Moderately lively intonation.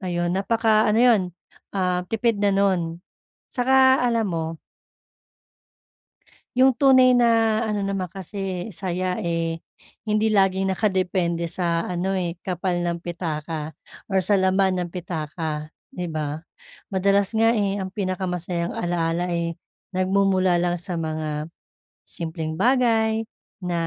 Yes: average, 3.4 semitones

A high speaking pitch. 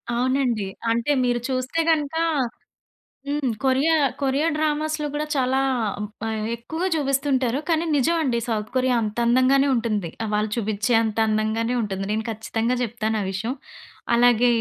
Yes: very high, 250 Hz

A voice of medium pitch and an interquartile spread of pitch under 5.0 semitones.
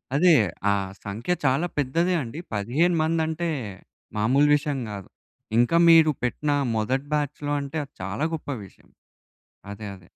No: medium, 145 Hz; average, 5.3 semitones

